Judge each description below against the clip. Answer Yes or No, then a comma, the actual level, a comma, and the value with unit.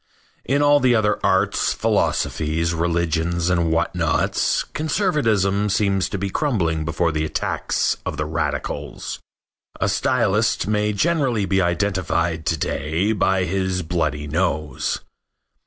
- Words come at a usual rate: No, slow, 125 wpm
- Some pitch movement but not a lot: Yes, average, 4.2 semitones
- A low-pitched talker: Yes, very low, 90 Hz